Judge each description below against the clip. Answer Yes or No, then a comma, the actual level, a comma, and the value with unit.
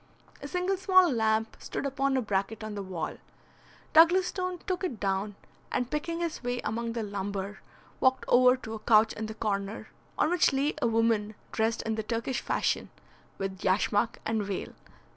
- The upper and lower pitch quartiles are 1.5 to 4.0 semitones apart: No, average, 4.8 semitones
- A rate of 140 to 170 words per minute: No, average, 180 wpm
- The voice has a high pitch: Yes, high, 225 Hz